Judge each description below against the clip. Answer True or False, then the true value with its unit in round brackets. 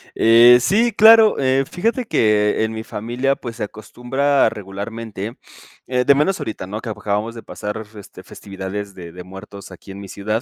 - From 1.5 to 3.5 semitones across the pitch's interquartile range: False (4.3 semitones)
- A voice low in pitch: True (110 Hz)